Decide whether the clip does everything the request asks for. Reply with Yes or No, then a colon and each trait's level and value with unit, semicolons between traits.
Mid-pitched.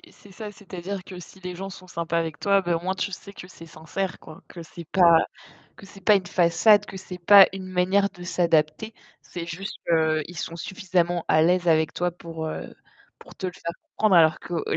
Yes: medium, 180 Hz